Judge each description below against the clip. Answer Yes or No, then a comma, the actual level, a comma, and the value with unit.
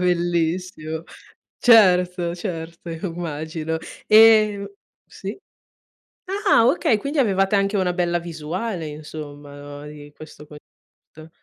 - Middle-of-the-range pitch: Yes, medium, 175 Hz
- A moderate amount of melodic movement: Yes, average, 4.1 semitones